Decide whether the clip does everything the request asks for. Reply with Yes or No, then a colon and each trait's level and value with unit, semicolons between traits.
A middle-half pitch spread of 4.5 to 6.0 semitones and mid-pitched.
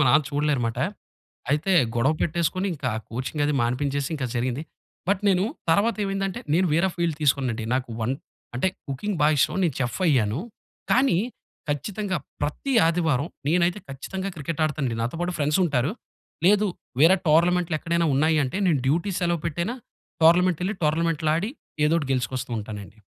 Yes: average, 4.8 semitones; medium, 155 Hz